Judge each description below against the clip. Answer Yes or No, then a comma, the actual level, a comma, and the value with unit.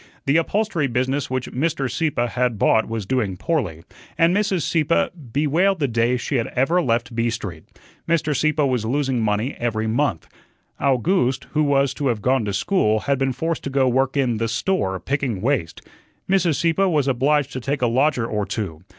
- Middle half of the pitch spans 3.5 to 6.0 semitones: Yes, average, 4.7 semitones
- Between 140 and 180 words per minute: No, average, 190 wpm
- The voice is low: Yes, low, 130 Hz